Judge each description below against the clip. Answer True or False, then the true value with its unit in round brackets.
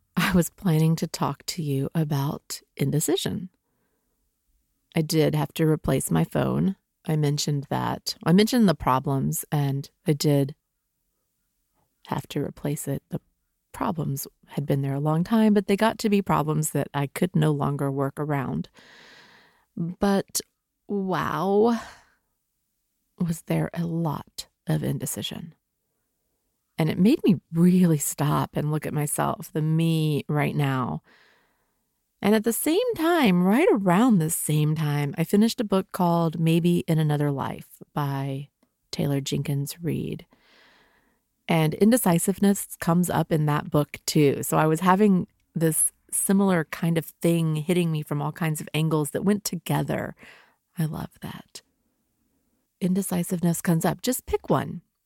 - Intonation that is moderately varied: True (4.4 semitones)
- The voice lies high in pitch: False (165 Hz)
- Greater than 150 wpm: False (145 wpm)